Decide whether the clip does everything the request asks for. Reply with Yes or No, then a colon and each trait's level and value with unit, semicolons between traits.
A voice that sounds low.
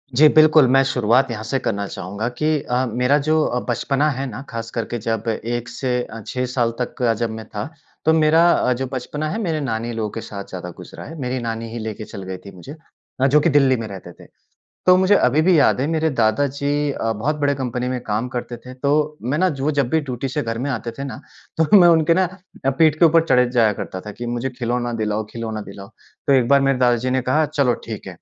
Yes: low, 125 Hz